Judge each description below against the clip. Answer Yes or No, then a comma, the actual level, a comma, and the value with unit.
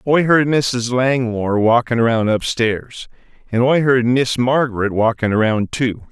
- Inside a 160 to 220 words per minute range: No, average, 145 wpm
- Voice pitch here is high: No, low, 120 Hz